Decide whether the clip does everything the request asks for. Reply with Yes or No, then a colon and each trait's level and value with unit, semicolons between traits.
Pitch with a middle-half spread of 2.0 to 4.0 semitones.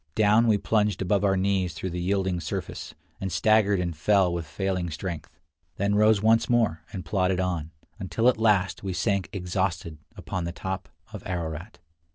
Yes: average, 2.8 semitones